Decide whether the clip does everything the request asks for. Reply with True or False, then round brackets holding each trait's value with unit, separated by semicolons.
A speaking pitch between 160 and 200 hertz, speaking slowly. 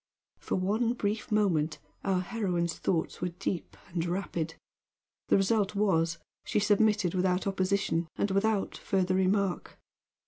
True (190 Hz; 130 wpm)